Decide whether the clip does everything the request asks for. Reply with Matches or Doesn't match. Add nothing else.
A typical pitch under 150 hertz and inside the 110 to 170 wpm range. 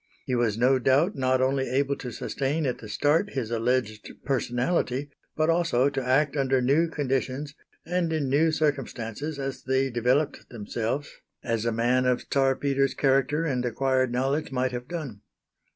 Matches